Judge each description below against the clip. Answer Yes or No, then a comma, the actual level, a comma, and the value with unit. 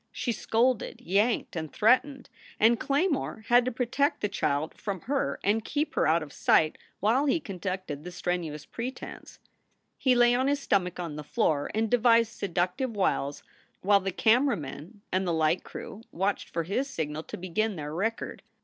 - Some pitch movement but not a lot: No, wide, 6.4 semitones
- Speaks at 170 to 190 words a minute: Yes, average, 175 wpm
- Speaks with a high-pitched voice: Yes, high, 205 Hz